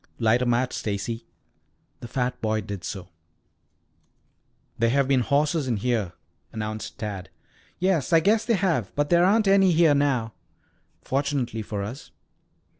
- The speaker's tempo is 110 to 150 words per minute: Yes, average, 145 wpm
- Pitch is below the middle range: Yes, low, 125 Hz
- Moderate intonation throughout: No, wide, 6.2 semitones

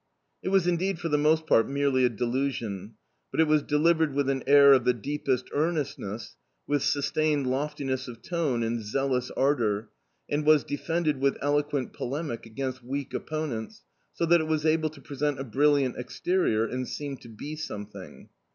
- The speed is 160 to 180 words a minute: Yes, average, 170 wpm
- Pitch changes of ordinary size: Yes, average, 3.5 semitones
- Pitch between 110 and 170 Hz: Yes, medium, 140 Hz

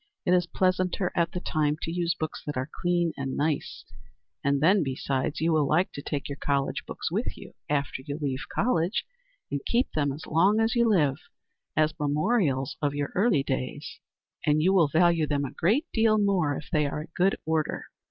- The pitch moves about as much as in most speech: Yes, average, 4.1 semitones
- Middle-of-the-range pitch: Yes, medium, 155 Hz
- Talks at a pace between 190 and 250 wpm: Yes, average, 200 wpm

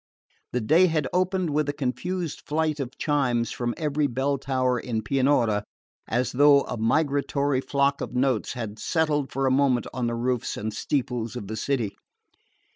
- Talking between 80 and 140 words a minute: No, average, 170 wpm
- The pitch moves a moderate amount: Yes, average, 3.3 semitones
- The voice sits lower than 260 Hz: Yes, low, 135 Hz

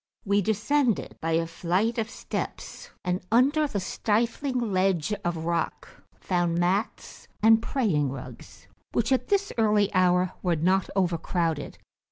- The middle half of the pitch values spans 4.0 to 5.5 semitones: Yes, average, 4.8 semitones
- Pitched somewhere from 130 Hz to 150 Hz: No, high, 190 Hz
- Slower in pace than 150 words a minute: Yes, slow, 135 wpm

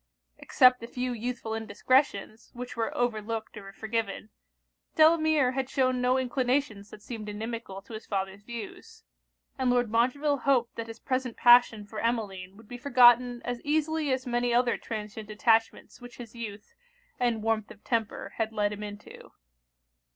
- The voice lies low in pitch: No, high, 235 Hz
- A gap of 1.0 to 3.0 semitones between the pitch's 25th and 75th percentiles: Yes, average, 2.7 semitones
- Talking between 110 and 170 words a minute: Yes, average, 160 wpm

